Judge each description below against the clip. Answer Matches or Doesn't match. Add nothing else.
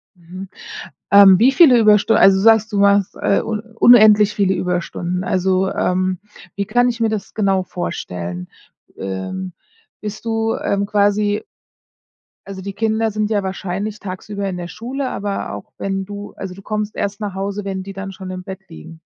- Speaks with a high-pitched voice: Matches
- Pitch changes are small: Matches